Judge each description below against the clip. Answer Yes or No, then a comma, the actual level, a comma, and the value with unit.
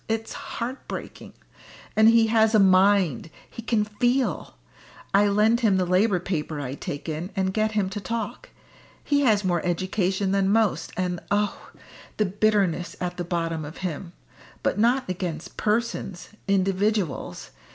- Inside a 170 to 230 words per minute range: No, average, 150 wpm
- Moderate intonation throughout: Yes, average, 3.5 semitones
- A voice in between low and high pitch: No, high, 195 Hz